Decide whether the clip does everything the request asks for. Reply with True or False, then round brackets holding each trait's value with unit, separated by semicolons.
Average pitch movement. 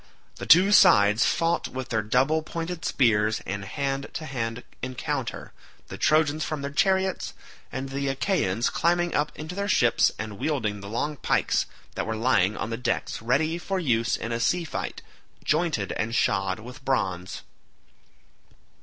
False (6.0 semitones)